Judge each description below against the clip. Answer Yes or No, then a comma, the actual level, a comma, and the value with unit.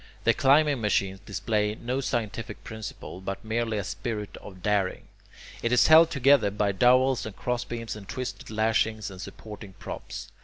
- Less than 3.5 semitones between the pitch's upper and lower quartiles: Yes, average, 3.1 semitones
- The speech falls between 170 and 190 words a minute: No, average, 155 wpm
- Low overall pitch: Yes, low, 110 Hz